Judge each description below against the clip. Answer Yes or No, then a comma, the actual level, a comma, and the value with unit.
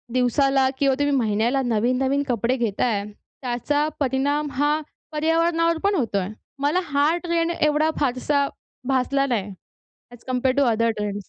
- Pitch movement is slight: No, average, 3.5 semitones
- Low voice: No, very high, 270 Hz